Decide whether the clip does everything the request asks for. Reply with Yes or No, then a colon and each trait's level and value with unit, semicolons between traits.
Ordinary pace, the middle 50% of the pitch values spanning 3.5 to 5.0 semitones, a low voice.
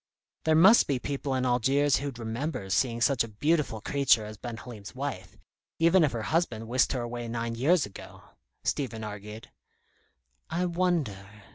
Yes: average, 160 wpm; average, 4.5 semitones; low, 125 Hz